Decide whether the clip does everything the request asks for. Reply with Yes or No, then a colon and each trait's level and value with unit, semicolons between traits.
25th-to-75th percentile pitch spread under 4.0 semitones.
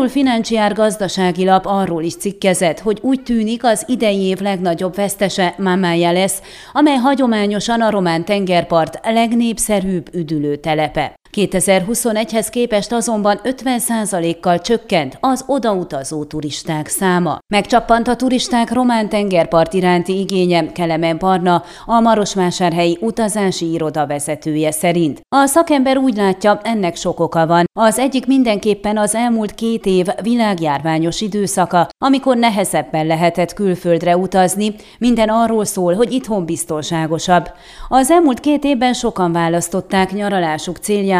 No: average, 4.9 semitones